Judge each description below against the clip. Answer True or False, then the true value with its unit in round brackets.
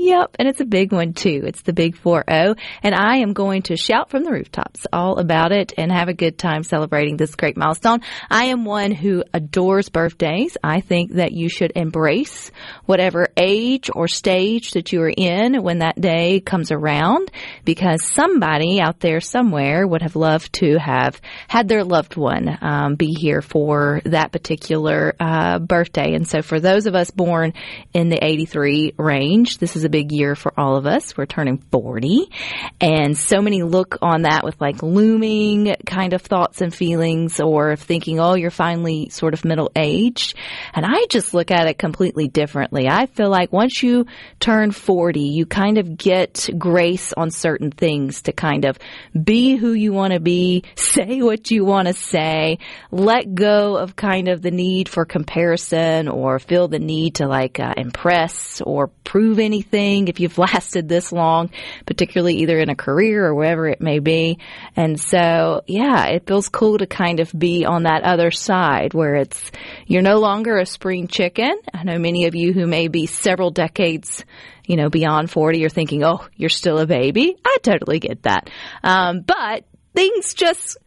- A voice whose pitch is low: False (175 Hz)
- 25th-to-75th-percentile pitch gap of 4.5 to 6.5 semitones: False (3.6 semitones)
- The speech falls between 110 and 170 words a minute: False (185 wpm)